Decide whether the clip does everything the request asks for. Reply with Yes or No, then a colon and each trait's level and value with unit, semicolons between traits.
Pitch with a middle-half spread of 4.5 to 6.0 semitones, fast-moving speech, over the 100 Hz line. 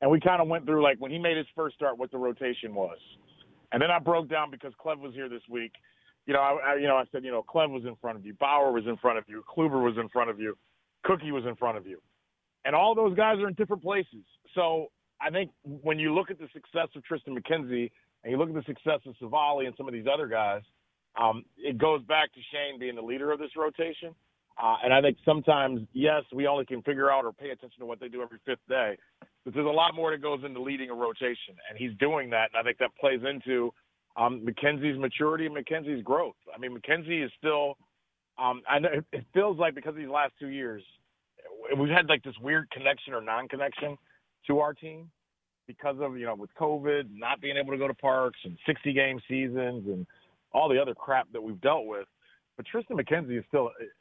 No: average, 4.0 semitones; fast, 240 wpm; medium, 140 Hz